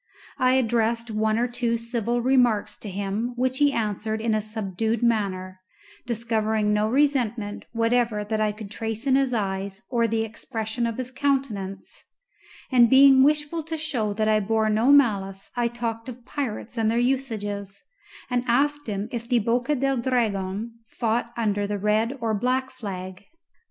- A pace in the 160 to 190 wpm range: Yes, average, 165 wpm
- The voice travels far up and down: No, average, 2.9 semitones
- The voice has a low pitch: No, high, 230 Hz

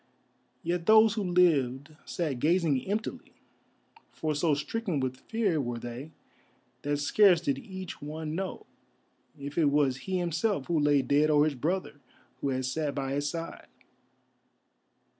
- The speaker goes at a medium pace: Yes, average, 145 wpm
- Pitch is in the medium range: Yes, medium, 155 Hz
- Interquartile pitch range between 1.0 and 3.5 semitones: No, average, 4.2 semitones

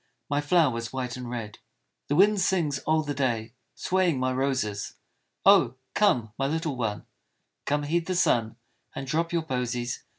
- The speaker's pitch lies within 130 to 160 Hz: Yes, low, 135 Hz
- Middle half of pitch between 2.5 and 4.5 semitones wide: No, average, 5.3 semitones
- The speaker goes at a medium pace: Yes, average, 175 wpm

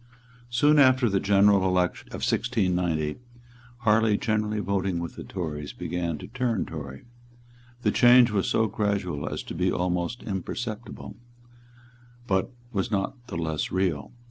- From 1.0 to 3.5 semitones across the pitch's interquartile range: No, average, 4.2 semitones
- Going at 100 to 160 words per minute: Yes, average, 140 wpm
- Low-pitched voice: Yes, low, 100 Hz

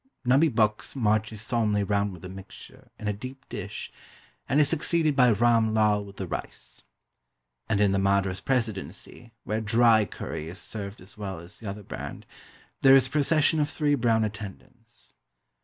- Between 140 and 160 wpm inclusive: No, average, 175 wpm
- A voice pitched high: No, low, 110 Hz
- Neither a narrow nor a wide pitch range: Yes, average, 3.8 semitones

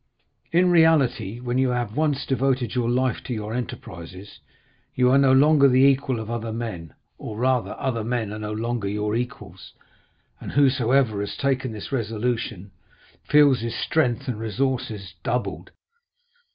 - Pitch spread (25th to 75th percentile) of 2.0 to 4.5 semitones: Yes, average, 3.6 semitones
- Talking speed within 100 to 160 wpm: Yes, average, 150 wpm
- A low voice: Yes, low, 120 Hz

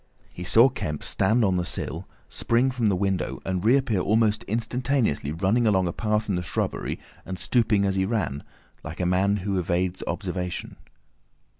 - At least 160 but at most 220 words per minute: Yes, average, 170 wpm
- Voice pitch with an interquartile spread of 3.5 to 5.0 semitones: Yes, average, 3.8 semitones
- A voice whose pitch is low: Yes, low, 100 Hz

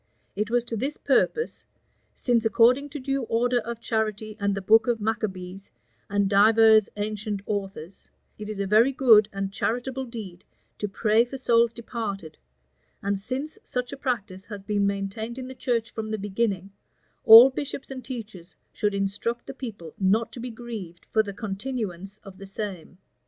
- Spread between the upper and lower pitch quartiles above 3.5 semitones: No, average, 3.2 semitones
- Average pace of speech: Yes, average, 170 wpm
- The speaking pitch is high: Yes, high, 220 Hz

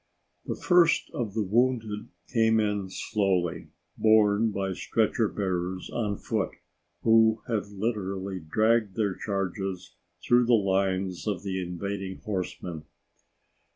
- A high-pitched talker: No, low, 100 Hz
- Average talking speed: No, slow, 115 wpm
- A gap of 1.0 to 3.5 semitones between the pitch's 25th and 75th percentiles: Yes, average, 2.9 semitones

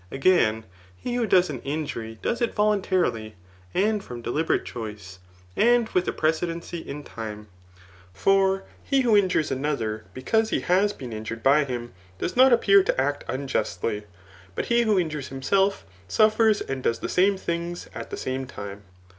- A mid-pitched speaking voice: Yes, medium, 155 Hz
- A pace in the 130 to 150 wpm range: No, average, 170 wpm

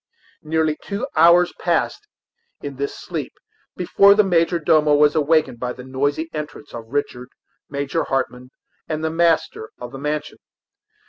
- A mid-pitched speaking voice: Yes, medium, 150 Hz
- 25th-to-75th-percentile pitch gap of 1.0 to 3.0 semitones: No, average, 3.4 semitones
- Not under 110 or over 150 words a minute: Yes, average, 145 wpm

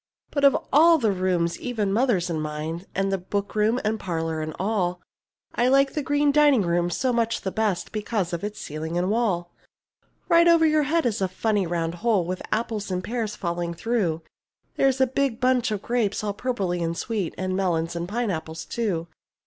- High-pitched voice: Yes, high, 205 Hz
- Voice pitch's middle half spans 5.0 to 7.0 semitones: Yes, wide, 5.6 semitones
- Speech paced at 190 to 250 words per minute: Yes, average, 195 wpm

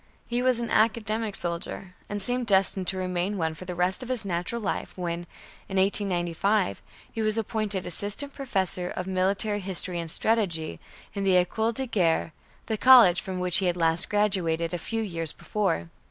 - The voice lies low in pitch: No, high, 190 Hz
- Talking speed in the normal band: Yes, average, 180 wpm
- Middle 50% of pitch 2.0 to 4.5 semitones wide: Yes, average, 3.6 semitones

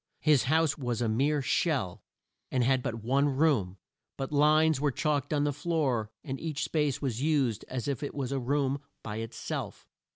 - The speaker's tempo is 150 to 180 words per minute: No, average, 190 wpm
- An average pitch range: Yes, average, 3.4 semitones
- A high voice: No, medium, 140 Hz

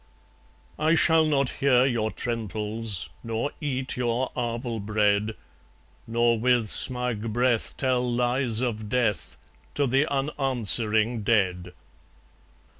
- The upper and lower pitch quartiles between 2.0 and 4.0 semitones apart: Yes, average, 2.8 semitones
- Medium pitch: No, low, 120 Hz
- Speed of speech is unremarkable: No, slow, 110 wpm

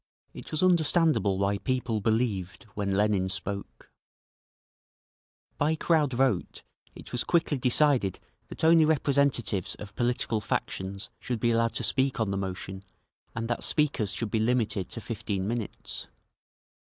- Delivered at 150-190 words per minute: No, average, 140 wpm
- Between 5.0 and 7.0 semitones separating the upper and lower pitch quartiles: Yes, wide, 5.5 semitones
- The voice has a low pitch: Yes, low, 115 Hz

